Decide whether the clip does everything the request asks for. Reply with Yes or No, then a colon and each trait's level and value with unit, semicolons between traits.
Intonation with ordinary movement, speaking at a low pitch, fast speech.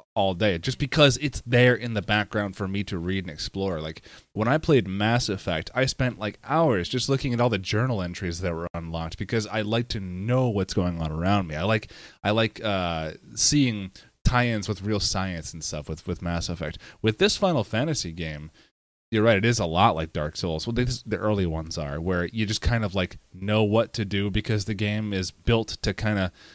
Yes: average, 4.6 semitones; low, 105 Hz; fast, 225 wpm